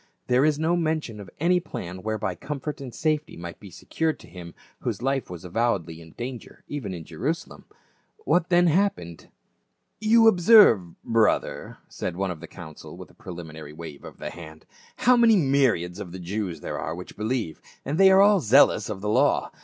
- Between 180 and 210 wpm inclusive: Yes, average, 190 wpm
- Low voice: Yes, low, 110 Hz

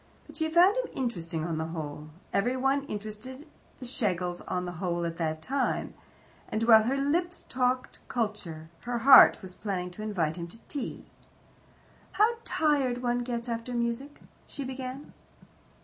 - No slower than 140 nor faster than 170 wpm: Yes, average, 160 wpm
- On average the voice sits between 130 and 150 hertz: No, high, 235 Hz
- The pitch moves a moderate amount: No, wide, 6.9 semitones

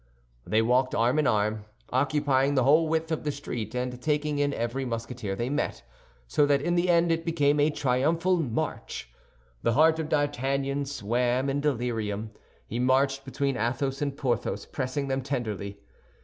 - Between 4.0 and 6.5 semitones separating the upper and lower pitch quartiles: No, average, 3.3 semitones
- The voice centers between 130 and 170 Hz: Yes, low, 135 Hz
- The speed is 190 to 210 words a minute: No, average, 165 wpm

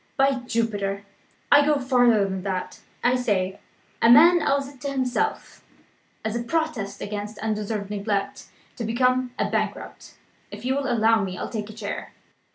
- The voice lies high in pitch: Yes, high, 230 Hz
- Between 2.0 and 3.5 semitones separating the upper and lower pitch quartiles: No, average, 4.3 semitones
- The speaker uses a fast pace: No, average, 165 wpm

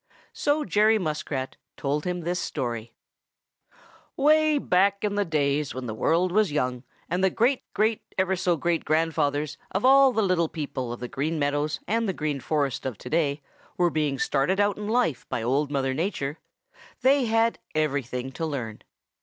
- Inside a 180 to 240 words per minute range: No, average, 170 wpm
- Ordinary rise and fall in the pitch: No, wide, 6.3 semitones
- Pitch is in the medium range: Yes, medium, 160 Hz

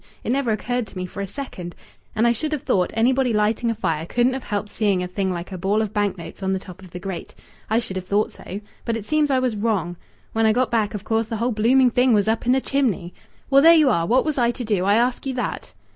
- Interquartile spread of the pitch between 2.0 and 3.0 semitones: No, average, 4.3 semitones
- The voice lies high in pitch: Yes, high, 220 Hz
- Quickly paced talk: Yes, fast, 275 wpm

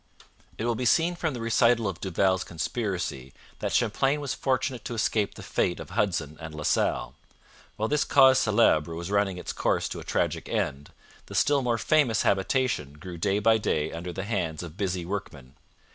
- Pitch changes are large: Yes, wide, 5.8 semitones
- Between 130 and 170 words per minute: No, average, 190 wpm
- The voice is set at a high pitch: No, low, 100 Hz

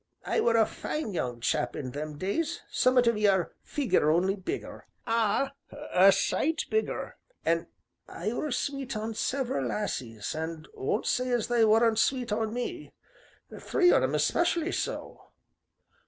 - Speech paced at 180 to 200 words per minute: No, average, 155 wpm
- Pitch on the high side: Yes, high, 220 Hz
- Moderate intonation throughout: No, wide, 7.4 semitones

